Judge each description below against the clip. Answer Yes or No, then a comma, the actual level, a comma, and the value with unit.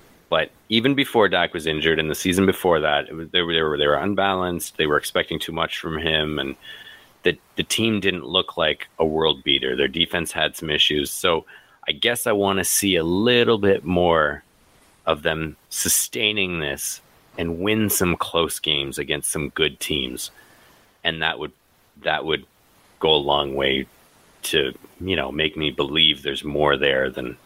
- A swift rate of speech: No, average, 180 wpm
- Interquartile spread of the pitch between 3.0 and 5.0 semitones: Yes, average, 4.5 semitones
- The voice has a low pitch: Yes, very low, 80 Hz